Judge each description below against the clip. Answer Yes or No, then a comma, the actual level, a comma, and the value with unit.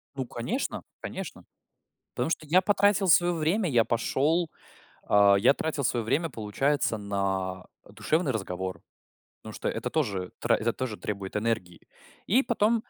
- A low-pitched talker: Yes, low, 130 Hz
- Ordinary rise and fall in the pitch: No, wide, 8.6 semitones